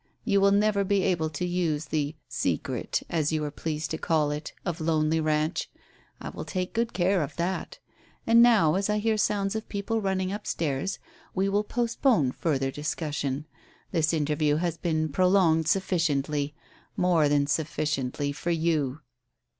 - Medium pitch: Yes, medium, 165 Hz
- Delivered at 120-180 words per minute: Yes, average, 160 wpm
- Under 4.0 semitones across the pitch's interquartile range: No, average, 4.3 semitones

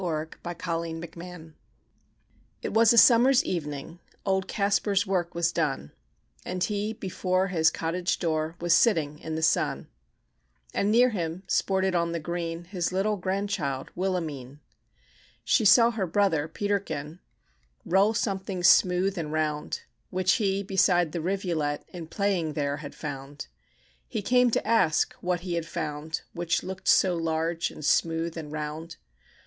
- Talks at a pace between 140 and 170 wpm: Yes, average, 145 wpm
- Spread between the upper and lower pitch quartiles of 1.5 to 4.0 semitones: Yes, average, 3.2 semitones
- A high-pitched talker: No, medium, 175 Hz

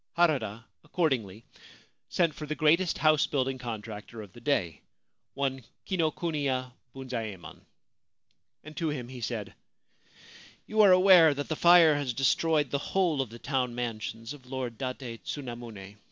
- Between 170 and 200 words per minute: No, average, 145 wpm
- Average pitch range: Yes, average, 4.8 semitones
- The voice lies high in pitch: No, low, 135 Hz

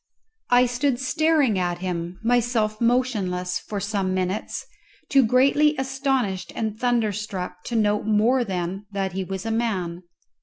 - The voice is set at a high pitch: Yes, high, 215 Hz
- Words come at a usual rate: Yes, average, 145 wpm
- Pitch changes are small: No, average, 4.8 semitones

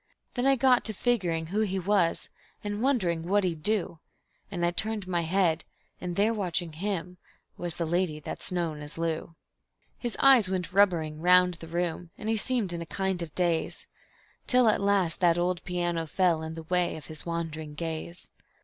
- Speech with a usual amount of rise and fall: Yes, average, 3.4 semitones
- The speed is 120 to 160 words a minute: No, average, 185 wpm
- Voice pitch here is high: No, medium, 175 Hz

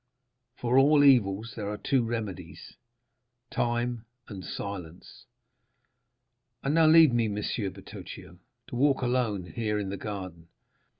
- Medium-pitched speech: No, low, 115 Hz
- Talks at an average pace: No, slow, 120 wpm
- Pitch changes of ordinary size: Yes, average, 3.8 semitones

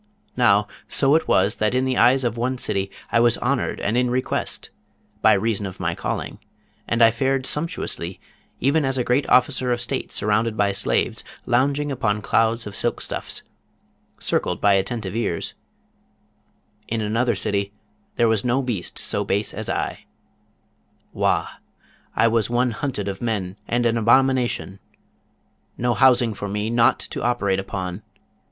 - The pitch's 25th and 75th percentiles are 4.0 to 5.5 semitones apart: No, average, 3.6 semitones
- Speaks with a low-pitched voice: Yes, low, 115 Hz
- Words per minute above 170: No, average, 160 wpm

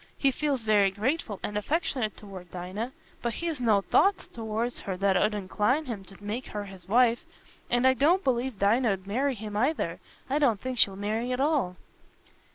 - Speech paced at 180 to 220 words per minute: Yes, average, 185 wpm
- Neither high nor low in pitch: No, high, 225 Hz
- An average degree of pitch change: Yes, average, 4.4 semitones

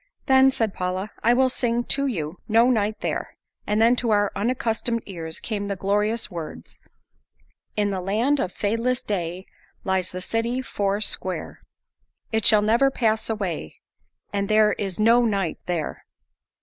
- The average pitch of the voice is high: Yes, high, 210 Hz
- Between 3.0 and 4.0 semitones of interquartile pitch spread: Yes, average, 3.4 semitones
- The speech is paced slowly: No, average, 155 wpm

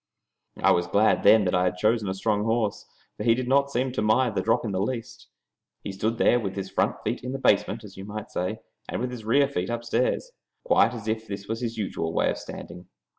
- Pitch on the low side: Yes, low, 110 Hz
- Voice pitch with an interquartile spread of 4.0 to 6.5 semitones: No, average, 3.3 semitones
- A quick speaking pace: Yes, fast, 240 wpm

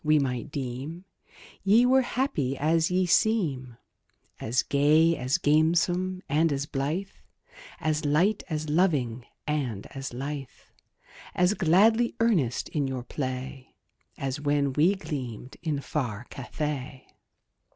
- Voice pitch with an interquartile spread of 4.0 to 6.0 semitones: Yes, average, 4.7 semitones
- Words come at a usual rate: No, slow, 120 wpm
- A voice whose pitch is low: No, medium, 150 Hz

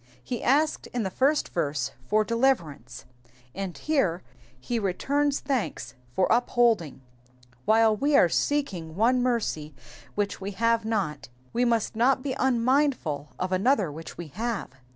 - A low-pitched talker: No, high, 225 Hz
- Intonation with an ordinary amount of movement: No, wide, 6.4 semitones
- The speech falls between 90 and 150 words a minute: Yes, average, 140 wpm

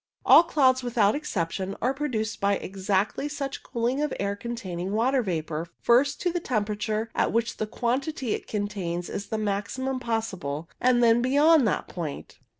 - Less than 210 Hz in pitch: No, high, 225 Hz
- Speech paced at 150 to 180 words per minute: Yes, average, 160 wpm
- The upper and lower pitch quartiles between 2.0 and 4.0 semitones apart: No, average, 4.5 semitones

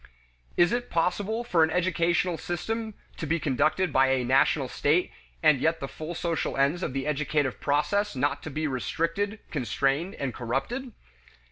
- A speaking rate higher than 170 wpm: No, average, 155 wpm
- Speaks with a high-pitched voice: No, medium, 160 Hz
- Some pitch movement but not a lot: Yes, average, 4.6 semitones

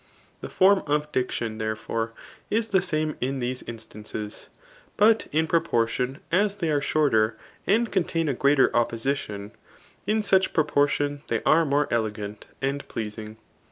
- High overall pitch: No, medium, 140 Hz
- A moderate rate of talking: Yes, average, 145 wpm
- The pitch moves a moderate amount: No, wide, 6.5 semitones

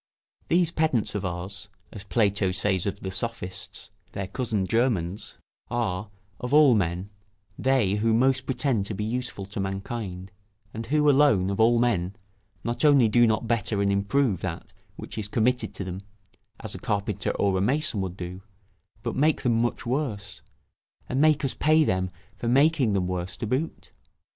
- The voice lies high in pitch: No, low, 110 Hz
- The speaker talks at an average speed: Yes, average, 170 wpm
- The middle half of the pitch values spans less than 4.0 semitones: No, average, 4.7 semitones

